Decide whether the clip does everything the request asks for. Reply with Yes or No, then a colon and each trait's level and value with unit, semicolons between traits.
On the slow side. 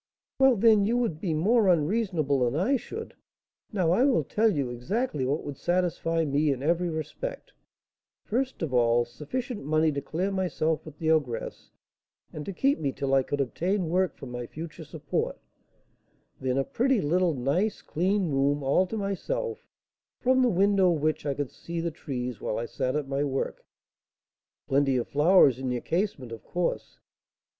No: average, 175 wpm